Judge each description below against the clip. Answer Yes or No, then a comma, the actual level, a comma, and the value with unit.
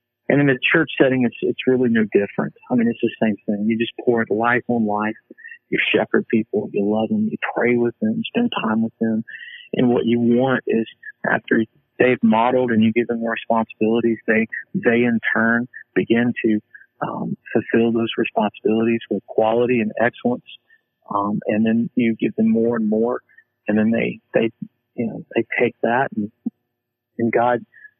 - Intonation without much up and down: Yes, narrow, 1.9 semitones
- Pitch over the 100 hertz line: Yes, low, 120 Hz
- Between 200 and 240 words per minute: No, average, 185 wpm